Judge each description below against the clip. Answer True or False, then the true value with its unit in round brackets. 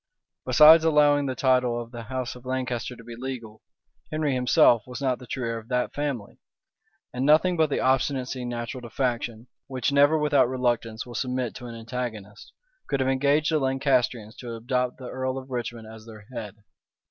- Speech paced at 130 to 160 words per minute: False (185 wpm)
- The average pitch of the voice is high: False (125 Hz)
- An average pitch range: False (2.2 semitones)